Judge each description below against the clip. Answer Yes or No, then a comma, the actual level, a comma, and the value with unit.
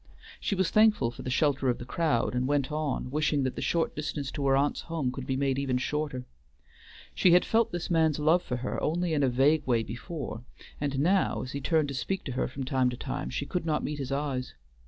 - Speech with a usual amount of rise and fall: Yes, average, 3.4 semitones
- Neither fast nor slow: No, fast, 240 wpm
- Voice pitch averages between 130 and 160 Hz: Yes, medium, 140 Hz